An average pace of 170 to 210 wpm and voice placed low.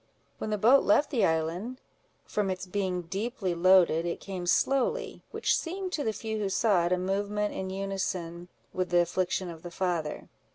No: average, 180 wpm; high, 190 Hz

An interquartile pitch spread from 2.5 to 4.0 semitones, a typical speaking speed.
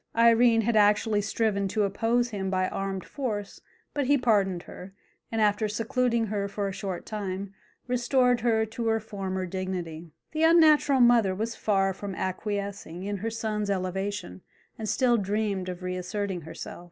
Yes: average, 3.0 semitones; average, 160 wpm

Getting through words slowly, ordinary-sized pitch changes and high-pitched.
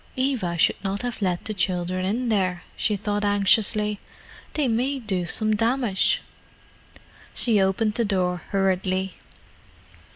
Yes: slow, 130 wpm; average, 3.3 semitones; high, 205 Hz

